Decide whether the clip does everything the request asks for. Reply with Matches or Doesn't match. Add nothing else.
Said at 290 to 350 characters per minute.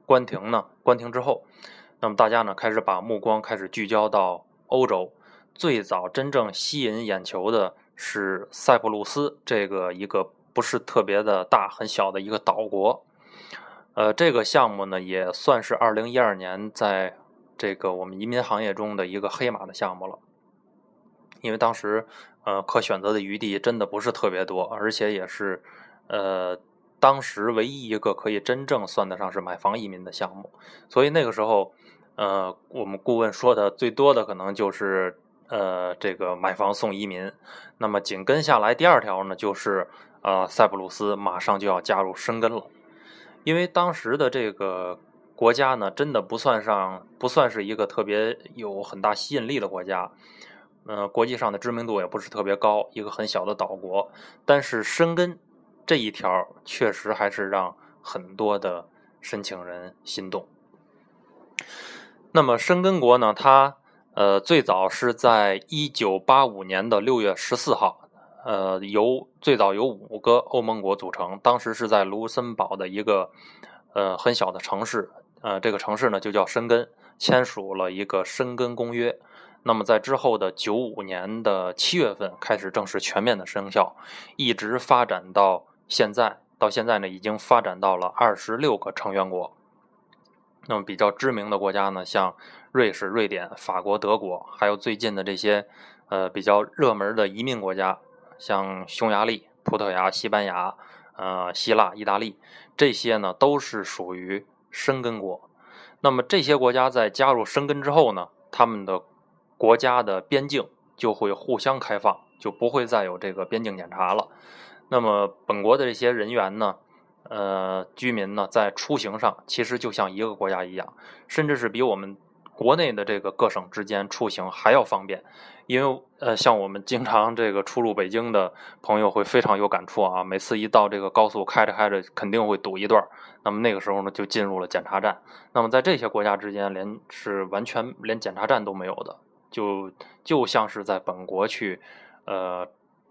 Doesn't match